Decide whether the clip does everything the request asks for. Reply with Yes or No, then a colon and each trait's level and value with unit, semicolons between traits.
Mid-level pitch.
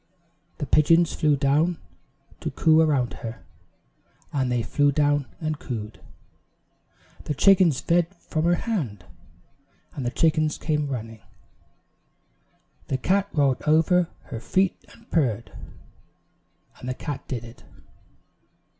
Yes: medium, 145 Hz